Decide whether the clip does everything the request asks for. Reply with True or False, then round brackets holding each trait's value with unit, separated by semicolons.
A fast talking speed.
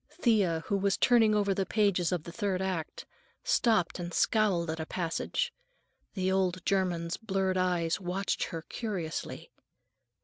False (145 wpm)